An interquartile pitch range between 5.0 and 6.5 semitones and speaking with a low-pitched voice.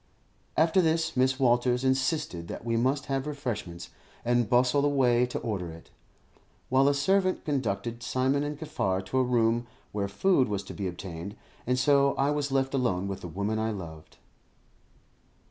Yes: wide, 5.6 semitones; low, 125 Hz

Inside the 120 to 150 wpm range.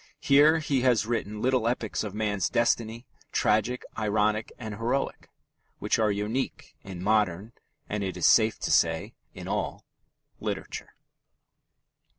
Yes: slow, 135 wpm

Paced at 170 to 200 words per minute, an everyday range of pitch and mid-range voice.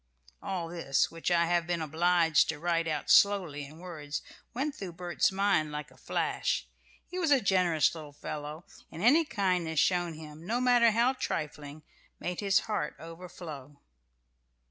No: average, 160 wpm; average, 4.0 semitones; medium, 170 Hz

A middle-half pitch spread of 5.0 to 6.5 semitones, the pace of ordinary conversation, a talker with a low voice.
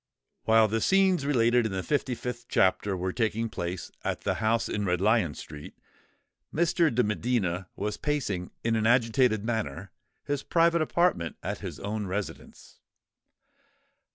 No: average, 4.2 semitones; average, 150 wpm; low, 110 Hz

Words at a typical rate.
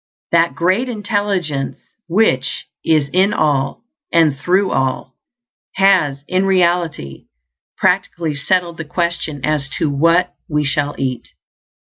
No: slow, 115 wpm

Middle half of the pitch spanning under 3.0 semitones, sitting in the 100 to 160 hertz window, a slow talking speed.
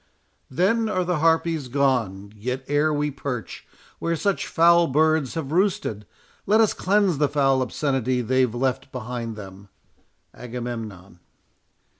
No: average, 5.3 semitones; low, 135 Hz; slow, 125 wpm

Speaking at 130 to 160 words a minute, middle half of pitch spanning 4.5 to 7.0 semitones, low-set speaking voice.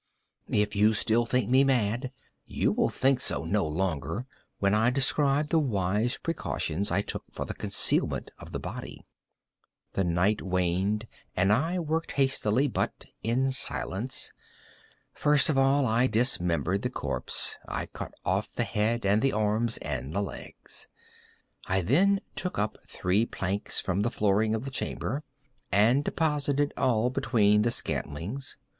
Yes: average, 150 wpm; average, 5.2 semitones; low, 110 Hz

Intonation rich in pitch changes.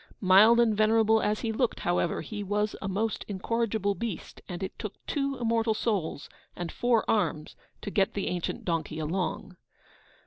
No: average, 3.4 semitones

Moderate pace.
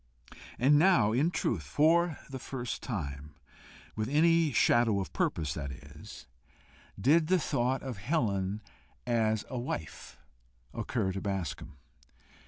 No: slow, 125 wpm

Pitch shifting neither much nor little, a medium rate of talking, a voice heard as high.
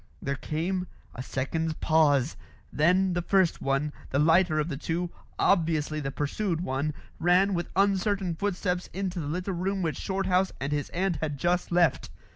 No: average, 3.7 semitones; average, 165 wpm; medium, 170 Hz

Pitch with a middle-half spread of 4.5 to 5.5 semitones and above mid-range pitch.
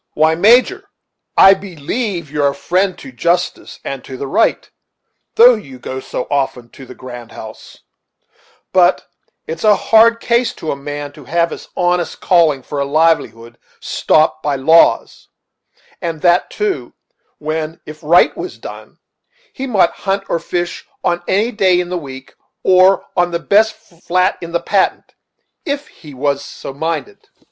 No: average, 5.2 semitones; medium, 170 Hz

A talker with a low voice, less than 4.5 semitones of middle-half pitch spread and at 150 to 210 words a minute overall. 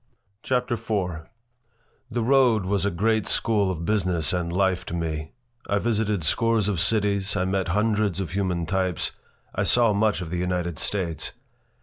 Yes: very low, 95 Hz; average, 3.5 semitones; average, 160 wpm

